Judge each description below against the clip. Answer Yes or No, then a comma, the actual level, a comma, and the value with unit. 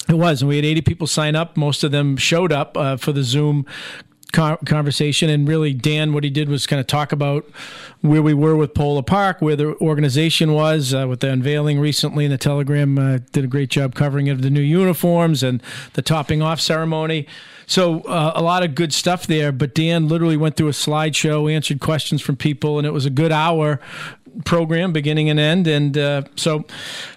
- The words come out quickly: Yes, fast, 210 wpm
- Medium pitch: Yes, medium, 150 Hz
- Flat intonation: Yes, narrow, 1.7 semitones